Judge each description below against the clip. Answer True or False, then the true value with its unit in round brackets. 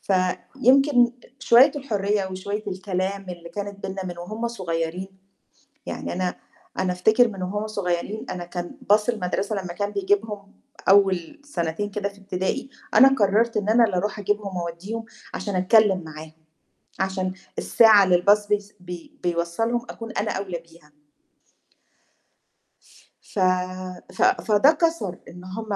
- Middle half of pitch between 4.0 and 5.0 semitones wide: False (3.1 semitones)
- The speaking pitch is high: True (200 Hz)